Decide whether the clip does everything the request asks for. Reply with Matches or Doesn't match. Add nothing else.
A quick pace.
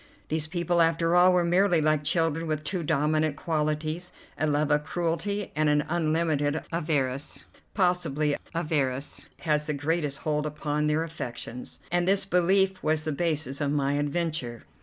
Doesn't match